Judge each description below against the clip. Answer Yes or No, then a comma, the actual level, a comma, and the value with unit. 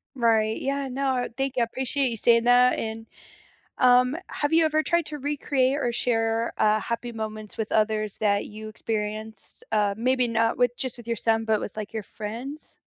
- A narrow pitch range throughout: No, average, 3.0 semitones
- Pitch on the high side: Yes, high, 235 Hz